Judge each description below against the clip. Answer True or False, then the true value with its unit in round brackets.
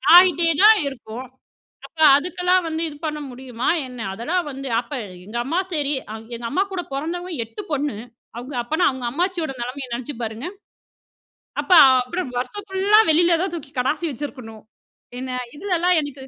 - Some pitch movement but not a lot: False (5.7 semitones)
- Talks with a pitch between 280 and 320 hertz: True (295 Hz)